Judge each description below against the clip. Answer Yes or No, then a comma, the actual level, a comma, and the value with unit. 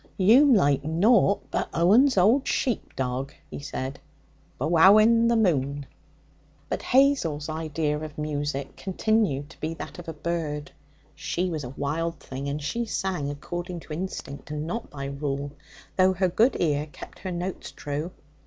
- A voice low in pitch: No, medium, 165 Hz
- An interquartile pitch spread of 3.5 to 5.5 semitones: Yes, average, 4.8 semitones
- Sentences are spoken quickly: No, average, 155 wpm